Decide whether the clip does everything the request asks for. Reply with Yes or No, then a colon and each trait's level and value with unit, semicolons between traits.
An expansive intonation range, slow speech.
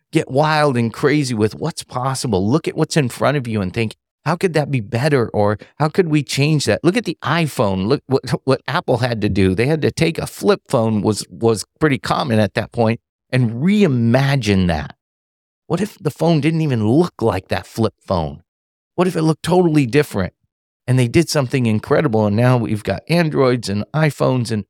No: wide, 6.2 semitones; fast, 205 wpm